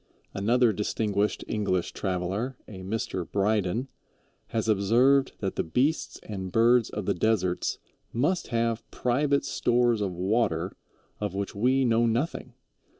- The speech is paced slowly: Yes, slow, 130 wpm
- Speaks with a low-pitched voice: Yes, low, 110 Hz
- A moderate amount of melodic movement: Yes, average, 3.8 semitones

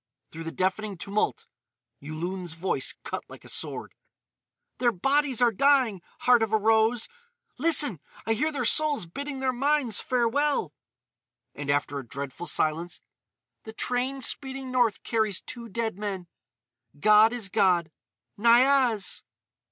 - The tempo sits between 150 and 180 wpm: No, slow, 135 wpm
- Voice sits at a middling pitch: No, high, 225 Hz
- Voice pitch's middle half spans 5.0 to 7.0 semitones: Yes, wide, 5.6 semitones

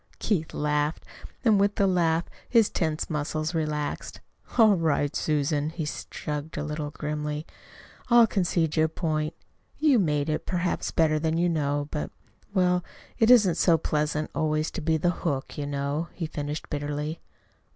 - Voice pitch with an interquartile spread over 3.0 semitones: No, average, 2.7 semitones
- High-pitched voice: No, medium, 155 Hz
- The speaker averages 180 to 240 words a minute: No, average, 155 wpm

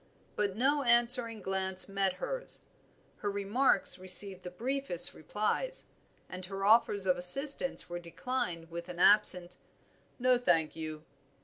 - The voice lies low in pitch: No, high, 195 Hz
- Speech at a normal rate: No, slow, 130 wpm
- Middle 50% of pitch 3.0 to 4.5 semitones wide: No, average, 5.2 semitones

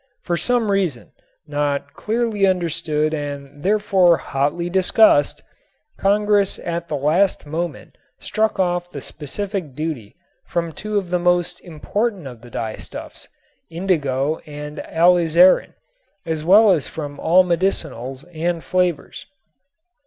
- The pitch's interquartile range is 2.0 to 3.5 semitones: No, average, 4.3 semitones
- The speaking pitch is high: No, medium, 170 Hz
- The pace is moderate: No, slow, 120 wpm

